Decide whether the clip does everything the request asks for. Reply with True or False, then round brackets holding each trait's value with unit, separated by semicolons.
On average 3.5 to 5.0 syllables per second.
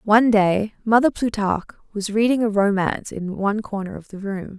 False (5.6 syllables/s)